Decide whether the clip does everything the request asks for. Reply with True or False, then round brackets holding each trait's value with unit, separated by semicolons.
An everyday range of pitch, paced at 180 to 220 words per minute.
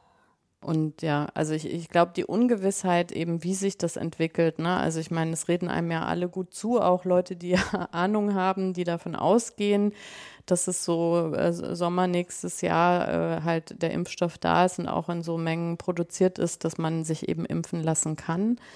False (2.0 semitones; 190 wpm)